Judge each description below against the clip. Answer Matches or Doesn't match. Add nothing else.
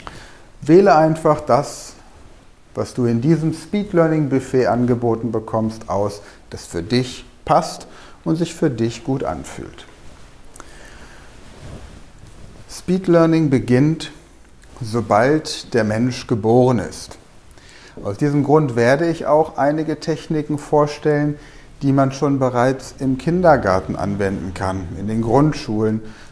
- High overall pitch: Doesn't match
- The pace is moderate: Doesn't match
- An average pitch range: Doesn't match